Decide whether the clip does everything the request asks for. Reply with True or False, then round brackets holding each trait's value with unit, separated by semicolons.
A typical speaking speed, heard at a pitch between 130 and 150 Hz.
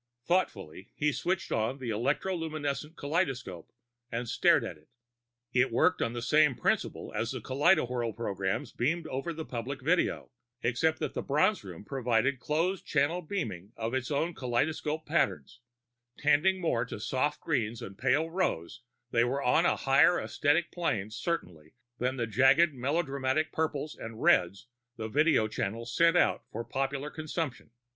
True (150 wpm; 135 Hz)